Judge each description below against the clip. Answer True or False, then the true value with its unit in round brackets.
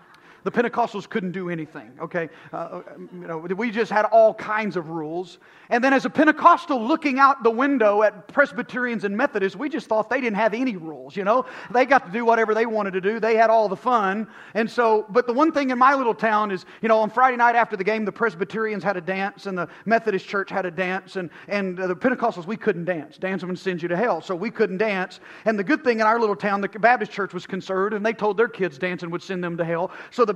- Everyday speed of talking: False (250 wpm)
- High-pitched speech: True (215 Hz)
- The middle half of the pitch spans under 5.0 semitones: True (3.8 semitones)